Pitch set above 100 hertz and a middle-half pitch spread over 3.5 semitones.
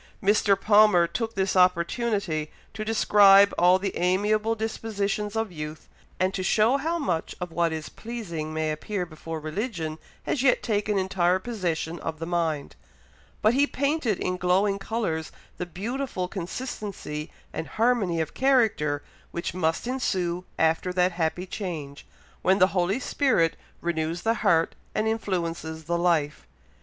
Yes: medium, 185 Hz; average, 4.5 semitones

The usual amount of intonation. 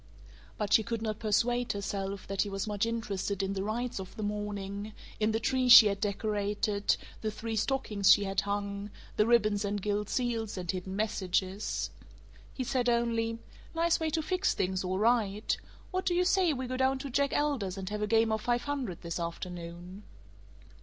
Yes: average, 3.3 semitones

